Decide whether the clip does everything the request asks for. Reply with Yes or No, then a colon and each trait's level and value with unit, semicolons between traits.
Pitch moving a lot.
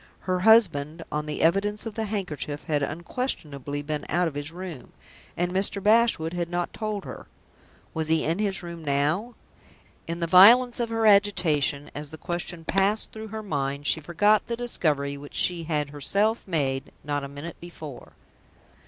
Yes: wide, 5.7 semitones